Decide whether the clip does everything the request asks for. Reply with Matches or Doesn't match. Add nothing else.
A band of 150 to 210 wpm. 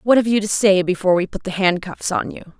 Doesn't match